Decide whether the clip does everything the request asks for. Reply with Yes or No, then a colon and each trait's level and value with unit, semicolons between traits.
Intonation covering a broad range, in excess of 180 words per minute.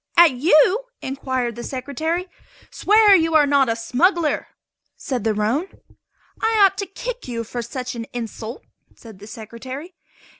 No: wide, 6.6 semitones; average, 150 wpm